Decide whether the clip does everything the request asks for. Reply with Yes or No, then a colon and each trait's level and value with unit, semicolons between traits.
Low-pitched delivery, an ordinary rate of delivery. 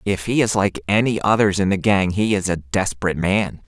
No: low, 100 Hz; fast, 230 wpm